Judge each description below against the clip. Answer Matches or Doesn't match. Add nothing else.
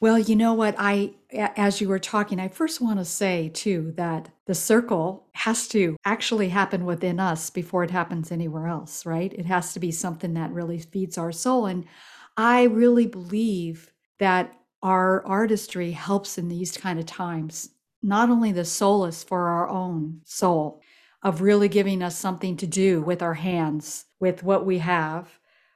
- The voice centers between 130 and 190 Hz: Matches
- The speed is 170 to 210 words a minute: Matches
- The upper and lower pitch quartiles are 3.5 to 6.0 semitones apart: Doesn't match